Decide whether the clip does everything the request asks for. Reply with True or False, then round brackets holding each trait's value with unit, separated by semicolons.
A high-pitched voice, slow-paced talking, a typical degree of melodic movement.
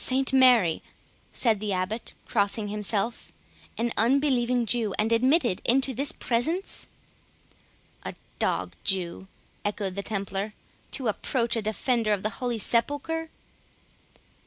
True (230 Hz; 120 wpm; 3.8 semitones)